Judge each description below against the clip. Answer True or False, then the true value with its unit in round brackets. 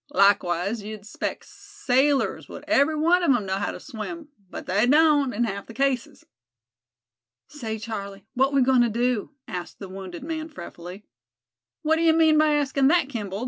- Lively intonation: True (6.8 semitones)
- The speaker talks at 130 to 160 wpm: False (175 wpm)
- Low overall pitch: False (250 Hz)